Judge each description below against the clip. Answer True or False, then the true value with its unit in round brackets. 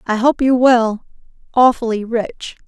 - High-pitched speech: True (235 Hz)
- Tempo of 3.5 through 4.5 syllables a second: True (4.0 syllables/s)